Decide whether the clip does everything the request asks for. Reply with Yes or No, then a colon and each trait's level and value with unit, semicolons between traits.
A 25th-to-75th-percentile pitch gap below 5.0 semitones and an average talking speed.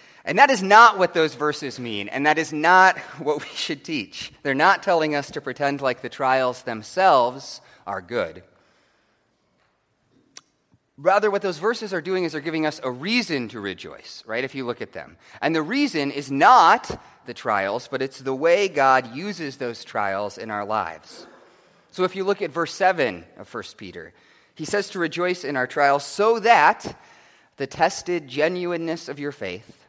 No: wide, 5.6 semitones; average, 185 wpm